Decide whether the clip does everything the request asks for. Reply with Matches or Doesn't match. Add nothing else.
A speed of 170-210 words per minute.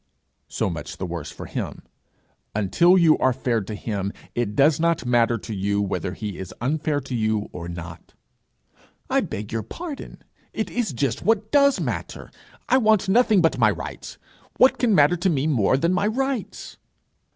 Matches